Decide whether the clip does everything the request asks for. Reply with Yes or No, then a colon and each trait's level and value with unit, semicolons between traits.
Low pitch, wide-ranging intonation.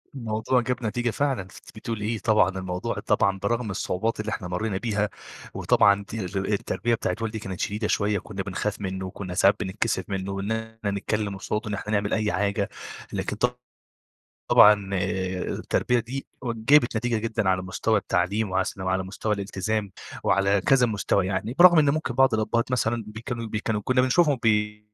No: low, 105 Hz; average, 2.8 semitones